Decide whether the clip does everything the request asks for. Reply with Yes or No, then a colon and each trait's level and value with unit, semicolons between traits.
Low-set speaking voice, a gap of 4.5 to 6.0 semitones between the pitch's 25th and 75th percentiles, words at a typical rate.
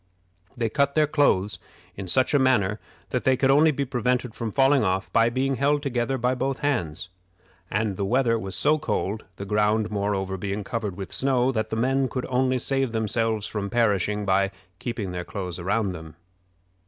Yes: low, 115 Hz; average, 4.8 semitones; average, 185 wpm